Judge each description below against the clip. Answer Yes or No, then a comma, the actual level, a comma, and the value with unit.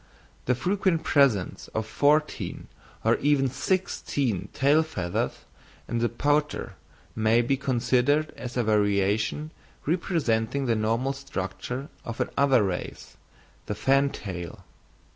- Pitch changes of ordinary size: Yes, average, 4.8 semitones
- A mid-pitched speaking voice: No, low, 125 Hz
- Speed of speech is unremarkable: No, slow, 110 wpm